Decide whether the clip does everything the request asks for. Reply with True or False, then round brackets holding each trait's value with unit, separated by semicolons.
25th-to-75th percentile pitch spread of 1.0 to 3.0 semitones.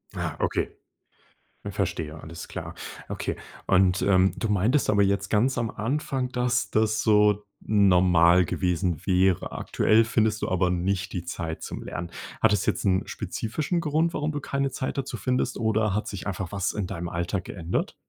False (3.9 semitones)